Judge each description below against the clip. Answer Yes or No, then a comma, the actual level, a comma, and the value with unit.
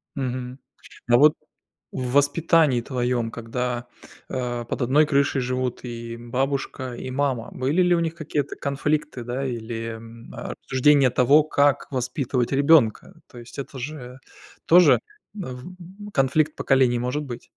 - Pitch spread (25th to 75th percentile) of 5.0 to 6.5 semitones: No, average, 3.1 semitones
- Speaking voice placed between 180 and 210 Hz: No, low, 130 Hz